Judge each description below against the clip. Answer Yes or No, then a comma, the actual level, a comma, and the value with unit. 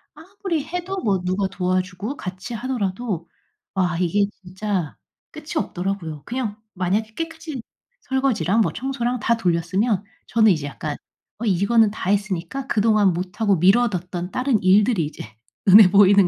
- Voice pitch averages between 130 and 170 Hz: No, high, 205 Hz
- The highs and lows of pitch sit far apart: No, average, 4.7 semitones